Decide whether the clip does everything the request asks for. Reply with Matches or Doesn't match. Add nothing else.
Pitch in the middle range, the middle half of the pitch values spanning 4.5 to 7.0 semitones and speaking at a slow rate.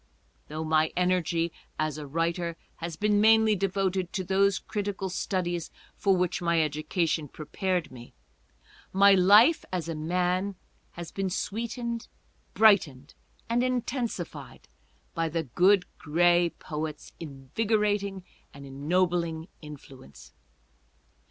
Doesn't match